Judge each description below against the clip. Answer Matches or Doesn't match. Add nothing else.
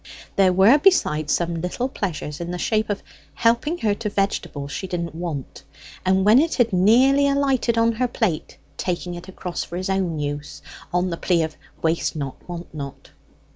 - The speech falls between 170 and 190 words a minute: Matches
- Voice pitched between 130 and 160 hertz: Doesn't match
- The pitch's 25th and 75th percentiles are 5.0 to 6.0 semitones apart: Matches